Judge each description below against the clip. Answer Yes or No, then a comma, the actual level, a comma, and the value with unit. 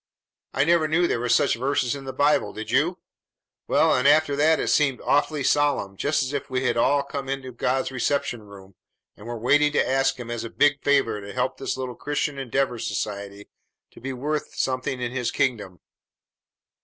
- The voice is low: Yes, low, 130 Hz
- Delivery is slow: No, average, 195 wpm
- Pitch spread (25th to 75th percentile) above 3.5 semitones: No, average, 3.2 semitones